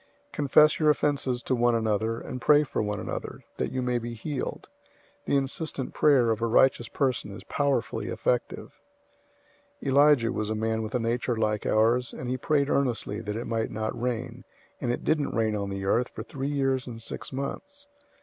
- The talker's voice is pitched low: Yes, low, 120 Hz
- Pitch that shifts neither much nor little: Yes, average, 3.6 semitones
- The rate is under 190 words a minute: No, average, 195 wpm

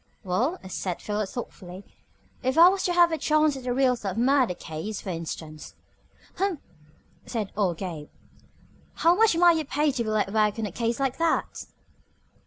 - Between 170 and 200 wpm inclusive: Yes, average, 180 wpm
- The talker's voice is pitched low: No, high, 235 Hz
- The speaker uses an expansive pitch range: Yes, wide, 8.0 semitones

